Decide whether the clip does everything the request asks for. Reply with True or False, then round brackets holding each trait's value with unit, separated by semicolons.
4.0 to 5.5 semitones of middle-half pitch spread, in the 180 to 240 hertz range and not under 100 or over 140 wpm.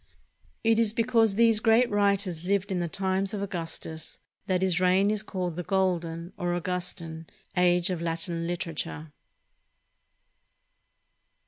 False (2.9 semitones; 185 Hz; 135 wpm)